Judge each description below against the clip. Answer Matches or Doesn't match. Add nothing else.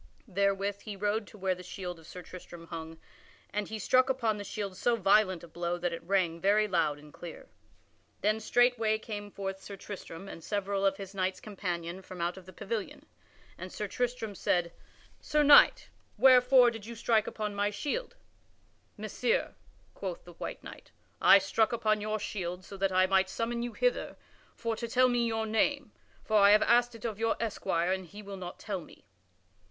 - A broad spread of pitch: Doesn't match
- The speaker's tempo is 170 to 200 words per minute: Matches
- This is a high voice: Matches